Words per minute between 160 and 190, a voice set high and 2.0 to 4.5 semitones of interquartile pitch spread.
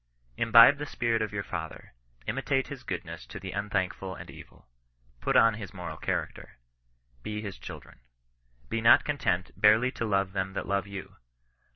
No: average, 165 wpm; low, 105 Hz; average, 3.2 semitones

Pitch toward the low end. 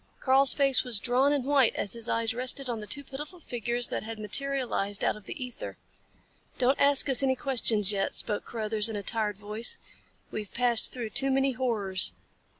No: high, 240 Hz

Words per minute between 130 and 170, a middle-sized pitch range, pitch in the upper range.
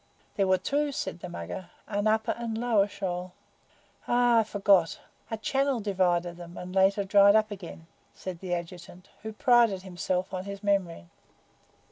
Yes: average, 165 wpm; average, 3.3 semitones; high, 195 Hz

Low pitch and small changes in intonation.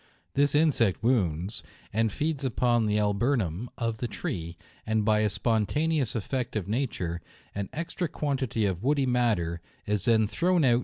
No: low, 115 Hz; average, 4.6 semitones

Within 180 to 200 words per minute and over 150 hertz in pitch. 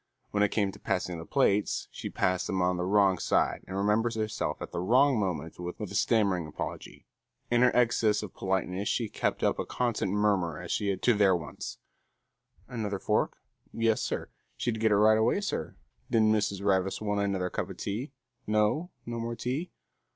No: average, 190 wpm; low, 105 Hz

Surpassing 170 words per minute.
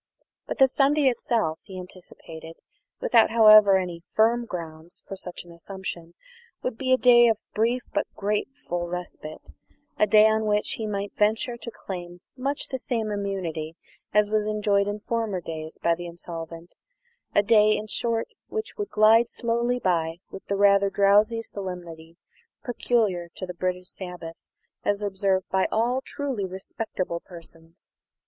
No: average, 155 wpm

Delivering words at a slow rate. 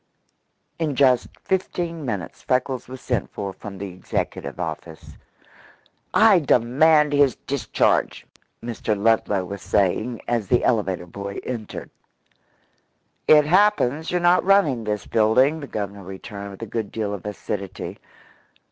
Yes: slow, 130 wpm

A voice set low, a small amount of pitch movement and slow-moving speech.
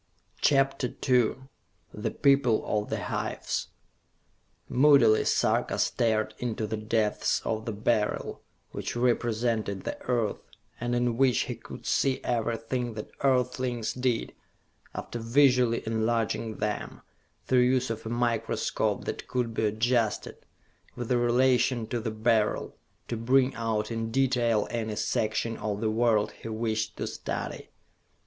Yes: low, 115 Hz; narrow, 2.1 semitones; slow, 130 wpm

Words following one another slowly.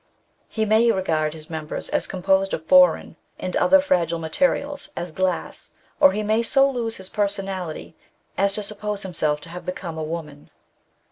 No: average, 165 wpm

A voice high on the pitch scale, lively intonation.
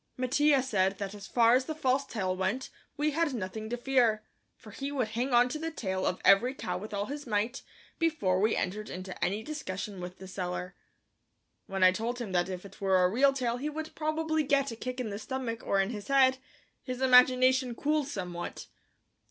Yes: high, 235 Hz; wide, 5.7 semitones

